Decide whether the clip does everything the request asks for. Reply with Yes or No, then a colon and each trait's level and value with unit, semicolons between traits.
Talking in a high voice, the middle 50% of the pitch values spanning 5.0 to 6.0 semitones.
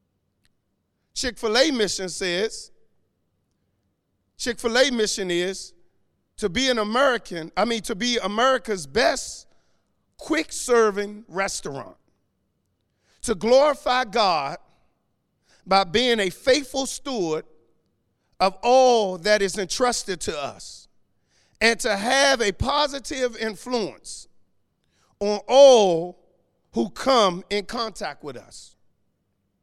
Yes: high, 215 Hz; wide, 5.5 semitones